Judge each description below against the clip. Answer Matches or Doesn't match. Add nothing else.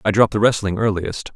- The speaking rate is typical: Doesn't match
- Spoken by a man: Matches